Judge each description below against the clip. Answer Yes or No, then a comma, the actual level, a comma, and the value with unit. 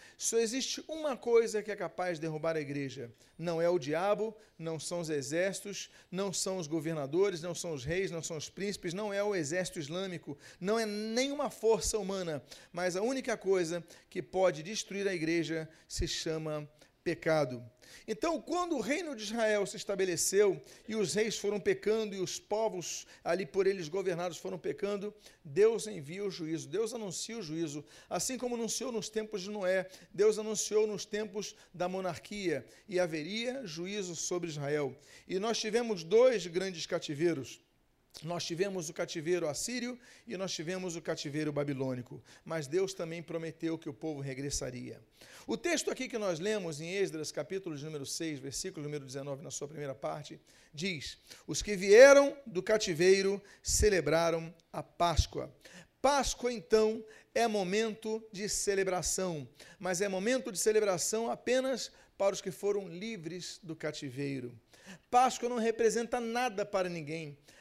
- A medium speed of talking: Yes, average, 160 wpm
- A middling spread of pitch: Yes, average, 4.8 semitones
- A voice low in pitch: No, medium, 185 Hz